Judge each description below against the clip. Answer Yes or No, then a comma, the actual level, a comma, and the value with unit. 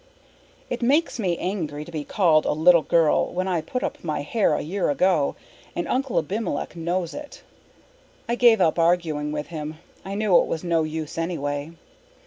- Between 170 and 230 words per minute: Yes, average, 180 wpm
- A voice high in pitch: No, medium, 170 Hz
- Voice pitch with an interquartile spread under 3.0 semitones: No, average, 3.9 semitones